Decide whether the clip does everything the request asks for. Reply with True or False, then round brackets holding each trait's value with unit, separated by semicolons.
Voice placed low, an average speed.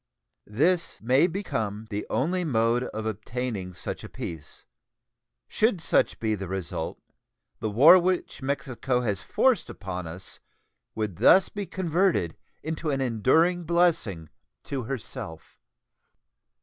False (125 Hz; 125 wpm)